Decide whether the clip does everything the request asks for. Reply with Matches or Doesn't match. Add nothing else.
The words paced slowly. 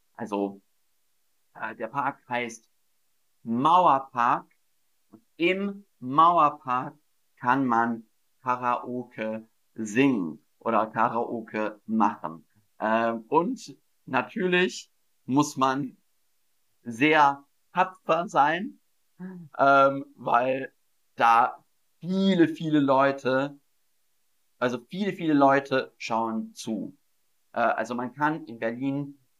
Matches